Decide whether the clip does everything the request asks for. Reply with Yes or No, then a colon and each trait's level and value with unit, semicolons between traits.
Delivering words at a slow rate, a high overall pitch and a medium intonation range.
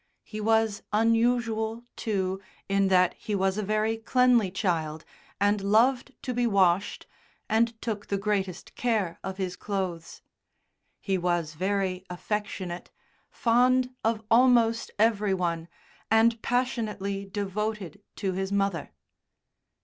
Yes: slow, 120 wpm; high, 205 Hz; average, 3.0 semitones